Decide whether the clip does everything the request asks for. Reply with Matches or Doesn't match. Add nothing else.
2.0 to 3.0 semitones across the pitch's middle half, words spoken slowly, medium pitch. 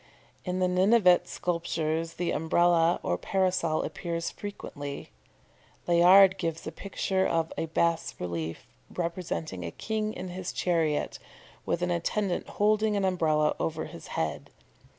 Matches